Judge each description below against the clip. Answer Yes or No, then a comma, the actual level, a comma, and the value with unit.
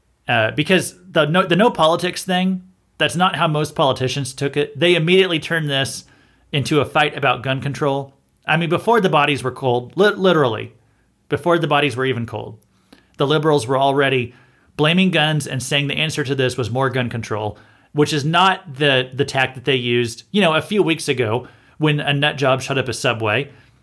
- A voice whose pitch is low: No, medium, 145 Hz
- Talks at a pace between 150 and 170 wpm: No, average, 200 wpm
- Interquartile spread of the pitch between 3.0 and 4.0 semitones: Yes, average, 3.7 semitones